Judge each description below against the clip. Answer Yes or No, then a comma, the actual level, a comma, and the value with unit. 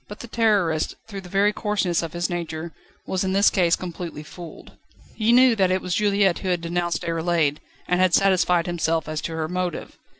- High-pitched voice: No, medium, 180 Hz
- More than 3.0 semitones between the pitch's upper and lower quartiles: No, average, 2.7 semitones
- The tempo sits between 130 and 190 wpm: No, average, 200 wpm